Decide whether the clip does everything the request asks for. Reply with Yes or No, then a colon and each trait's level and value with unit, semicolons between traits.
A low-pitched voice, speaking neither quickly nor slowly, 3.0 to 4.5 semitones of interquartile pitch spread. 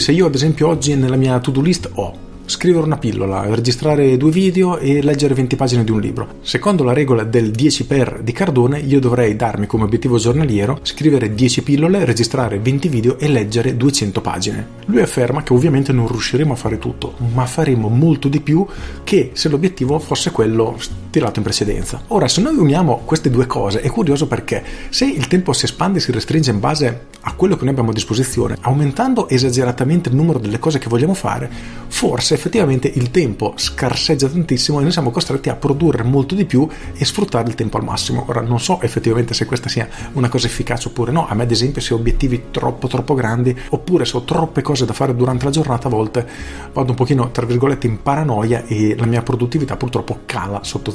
No: low, 130 Hz; fast, 205 wpm; average, 3.9 semitones